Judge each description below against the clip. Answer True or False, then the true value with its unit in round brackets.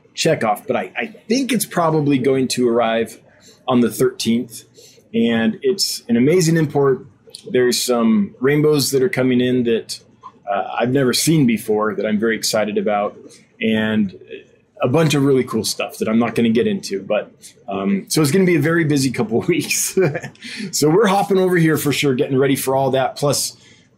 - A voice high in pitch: False (135 Hz)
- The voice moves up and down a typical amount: False (6.1 semitones)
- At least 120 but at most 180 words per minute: False (195 wpm)